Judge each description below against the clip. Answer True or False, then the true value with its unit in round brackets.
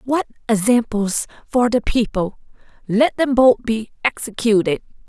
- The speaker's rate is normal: False (120 wpm)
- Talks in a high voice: True (230 Hz)